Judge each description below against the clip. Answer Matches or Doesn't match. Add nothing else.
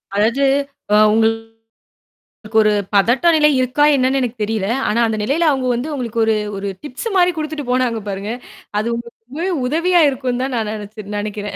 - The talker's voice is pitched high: Matches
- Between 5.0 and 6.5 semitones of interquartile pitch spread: Doesn't match